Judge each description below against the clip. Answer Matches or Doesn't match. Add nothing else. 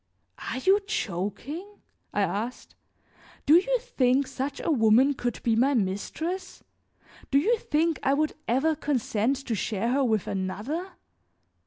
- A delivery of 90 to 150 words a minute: Matches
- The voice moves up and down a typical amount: Doesn't match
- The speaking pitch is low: Doesn't match